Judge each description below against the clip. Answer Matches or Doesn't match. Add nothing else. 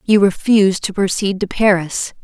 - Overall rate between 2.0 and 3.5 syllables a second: Doesn't match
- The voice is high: Matches